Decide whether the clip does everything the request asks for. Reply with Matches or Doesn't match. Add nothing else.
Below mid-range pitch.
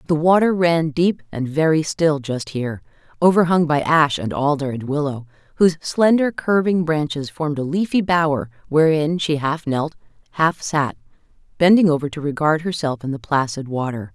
Doesn't match